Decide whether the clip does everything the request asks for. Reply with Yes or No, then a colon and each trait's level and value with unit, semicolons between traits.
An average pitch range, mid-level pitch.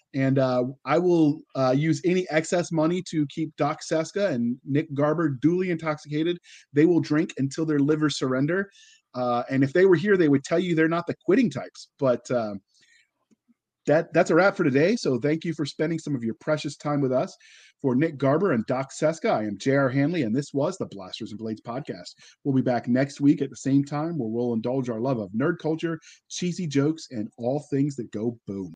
Yes: average, 3.5 semitones; medium, 150 Hz